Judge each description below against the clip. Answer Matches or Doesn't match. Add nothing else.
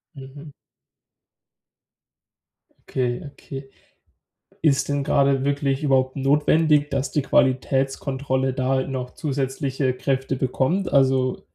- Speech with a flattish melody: Matches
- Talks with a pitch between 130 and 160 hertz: Matches